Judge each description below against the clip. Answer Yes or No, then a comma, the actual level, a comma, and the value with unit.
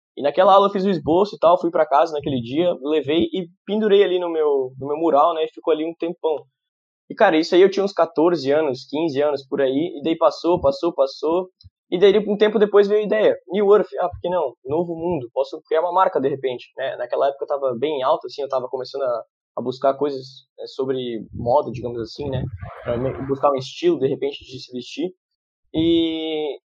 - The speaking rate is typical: No, fast, 225 wpm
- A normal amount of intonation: No, wide, 6.1 semitones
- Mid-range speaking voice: Yes, medium, 160 Hz